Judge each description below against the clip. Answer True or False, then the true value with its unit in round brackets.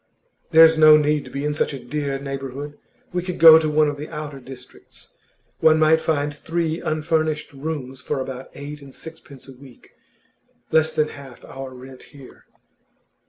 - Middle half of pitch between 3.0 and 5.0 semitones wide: False (2.6 semitones)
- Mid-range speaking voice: True (145 Hz)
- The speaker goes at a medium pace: True (170 wpm)